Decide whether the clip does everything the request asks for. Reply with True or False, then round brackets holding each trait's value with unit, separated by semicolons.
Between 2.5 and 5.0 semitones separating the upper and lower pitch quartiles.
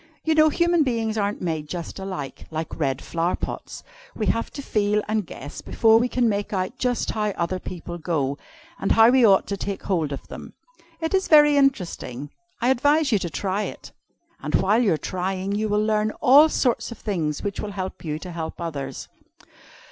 False (5.6 semitones)